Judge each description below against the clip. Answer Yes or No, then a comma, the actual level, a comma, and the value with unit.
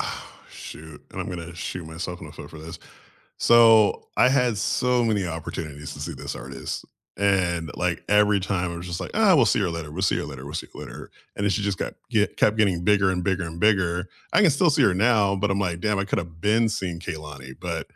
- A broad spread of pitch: No, average, 4.0 semitones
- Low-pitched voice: Yes, very low, 95 Hz